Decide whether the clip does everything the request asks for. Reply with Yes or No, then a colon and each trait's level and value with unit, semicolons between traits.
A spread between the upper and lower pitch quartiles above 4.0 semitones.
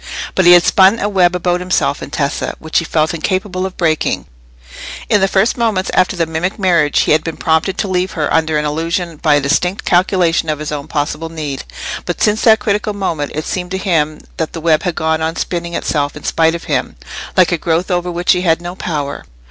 No: average, 2.8 semitones